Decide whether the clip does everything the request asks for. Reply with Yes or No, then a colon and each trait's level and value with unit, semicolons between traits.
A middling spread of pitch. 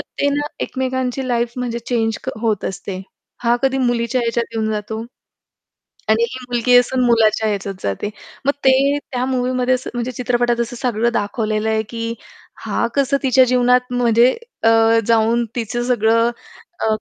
No: narrow, 2.1 semitones